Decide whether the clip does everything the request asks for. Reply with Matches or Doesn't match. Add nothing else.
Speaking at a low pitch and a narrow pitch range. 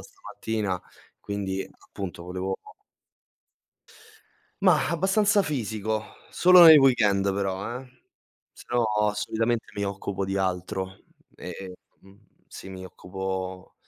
Doesn't match